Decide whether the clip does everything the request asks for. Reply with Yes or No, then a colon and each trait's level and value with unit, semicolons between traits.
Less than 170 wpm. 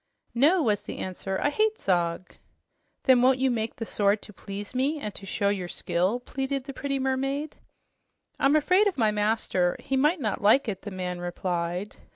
No: average, 190 wpm